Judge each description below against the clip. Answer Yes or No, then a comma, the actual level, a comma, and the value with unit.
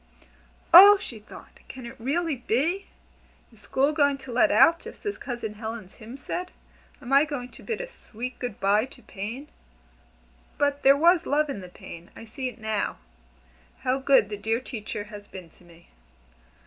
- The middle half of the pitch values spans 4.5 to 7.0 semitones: Yes, average, 5.1 semitones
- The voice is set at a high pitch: Yes, very high, 255 Hz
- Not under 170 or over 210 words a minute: Yes, average, 180 wpm